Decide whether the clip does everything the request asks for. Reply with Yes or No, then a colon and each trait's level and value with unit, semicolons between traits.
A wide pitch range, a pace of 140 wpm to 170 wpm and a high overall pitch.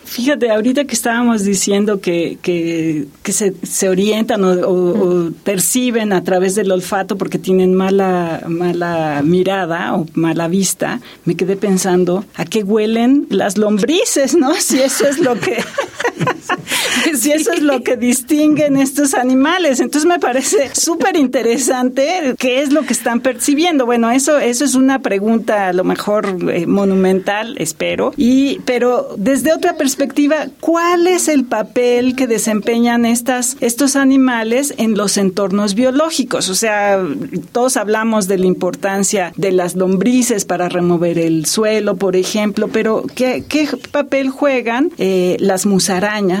Yes: wide, 5.8 semitones; average, 150 wpm; high, 225 Hz